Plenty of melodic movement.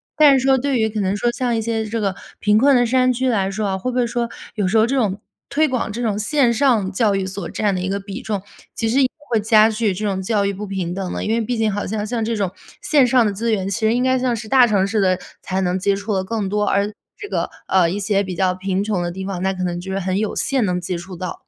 No: average, 3.5 semitones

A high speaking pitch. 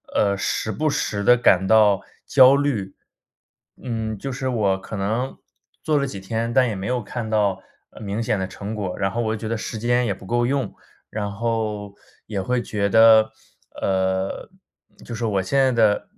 No: low, 110 Hz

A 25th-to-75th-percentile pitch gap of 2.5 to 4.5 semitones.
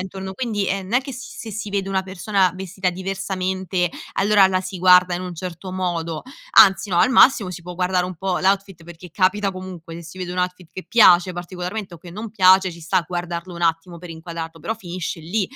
No: narrow, 1.8 semitones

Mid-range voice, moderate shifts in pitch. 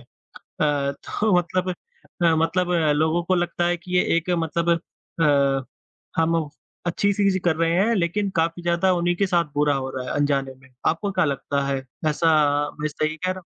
Yes: medium, 170 Hz; average, 3.3 semitones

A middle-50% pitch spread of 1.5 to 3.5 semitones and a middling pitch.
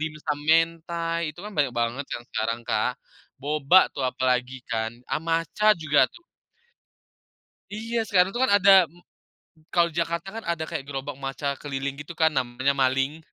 No: average, 4.1 semitones; medium, 150 Hz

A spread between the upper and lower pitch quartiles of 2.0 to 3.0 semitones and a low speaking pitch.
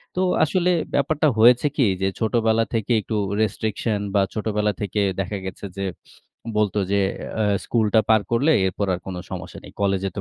Yes: narrow, 2.6 semitones; low, 110 Hz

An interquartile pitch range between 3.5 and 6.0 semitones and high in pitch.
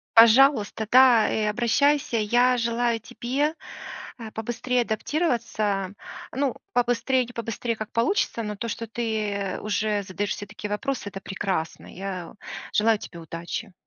No: average, 2.9 semitones; high, 225 Hz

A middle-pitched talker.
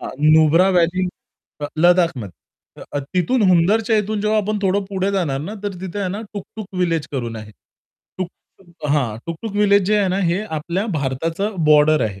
Yes: medium, 180 Hz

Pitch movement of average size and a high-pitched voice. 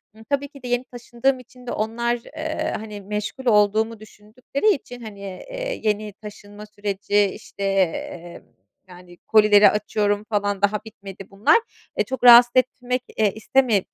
Yes: average, 3.2 semitones; high, 215 Hz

